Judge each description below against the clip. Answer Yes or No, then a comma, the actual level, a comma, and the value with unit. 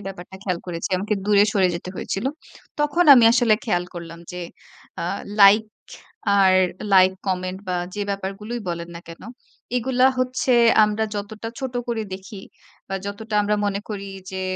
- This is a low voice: No, high, 200 Hz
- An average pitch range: Yes, average, 3.1 semitones